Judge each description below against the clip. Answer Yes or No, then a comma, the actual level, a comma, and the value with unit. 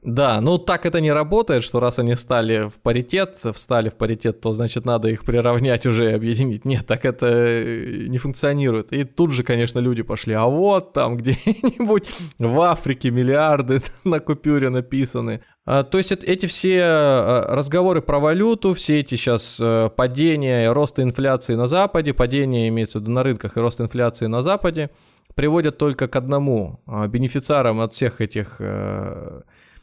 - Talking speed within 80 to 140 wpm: No, fast, 160 wpm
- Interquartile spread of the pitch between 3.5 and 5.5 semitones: Yes, average, 4.5 semitones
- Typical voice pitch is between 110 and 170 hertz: Yes, low, 130 Hz